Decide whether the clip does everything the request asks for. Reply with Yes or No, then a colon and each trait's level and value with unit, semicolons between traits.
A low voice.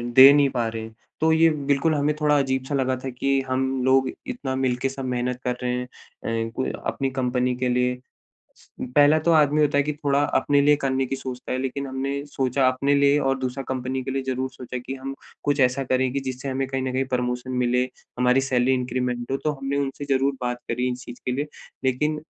Yes: low, 130 Hz